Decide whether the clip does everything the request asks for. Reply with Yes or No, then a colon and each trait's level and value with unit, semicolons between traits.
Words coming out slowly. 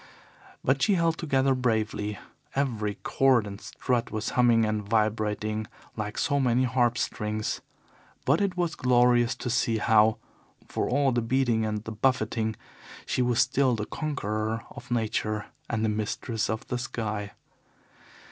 No: average, 145 wpm